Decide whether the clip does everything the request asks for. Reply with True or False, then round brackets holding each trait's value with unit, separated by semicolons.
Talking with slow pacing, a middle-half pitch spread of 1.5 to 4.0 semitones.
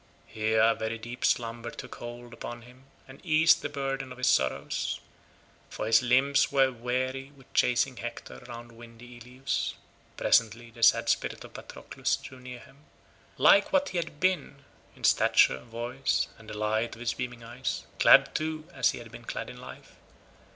False (175 wpm; 2.6 semitones)